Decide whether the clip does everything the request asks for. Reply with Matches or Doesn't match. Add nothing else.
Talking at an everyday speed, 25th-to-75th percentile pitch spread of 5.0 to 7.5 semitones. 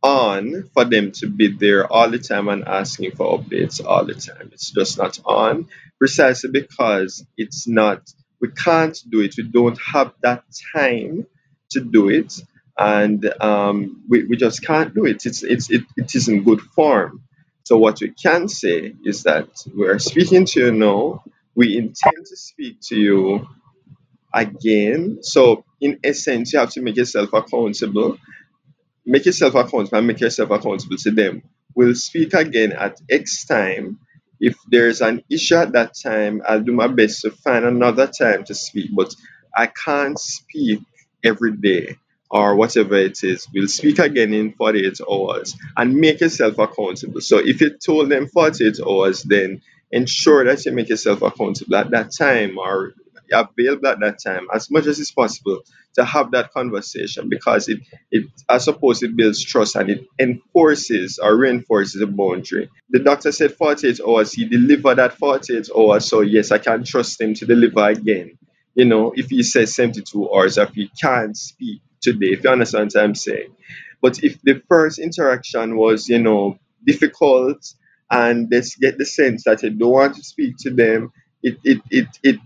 Matches